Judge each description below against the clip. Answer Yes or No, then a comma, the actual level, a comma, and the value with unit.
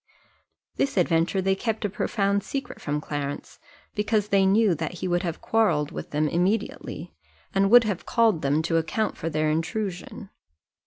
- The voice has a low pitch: No, high, 190 Hz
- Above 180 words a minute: No, average, 165 wpm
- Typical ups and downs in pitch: Yes, average, 4.7 semitones